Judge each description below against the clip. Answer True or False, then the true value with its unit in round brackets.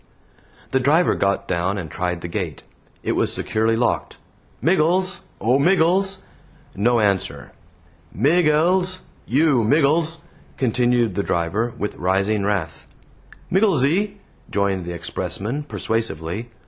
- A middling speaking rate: False (115 wpm)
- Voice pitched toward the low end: True (120 Hz)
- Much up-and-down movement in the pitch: True (8.5 semitones)